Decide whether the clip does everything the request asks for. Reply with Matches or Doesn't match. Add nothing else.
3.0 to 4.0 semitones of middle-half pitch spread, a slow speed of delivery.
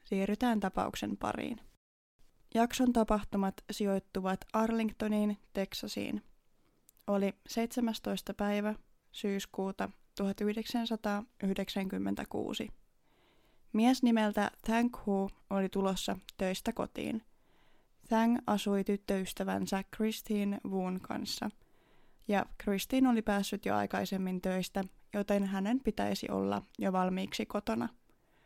Doesn't match